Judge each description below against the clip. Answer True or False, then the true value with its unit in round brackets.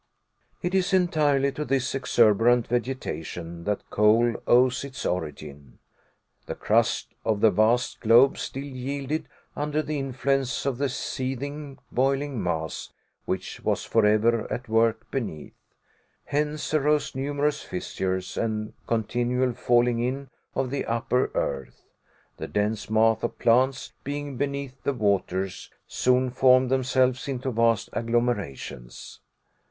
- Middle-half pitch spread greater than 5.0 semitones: False (3.7 semitones)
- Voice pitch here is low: True (125 Hz)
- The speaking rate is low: True (125 wpm)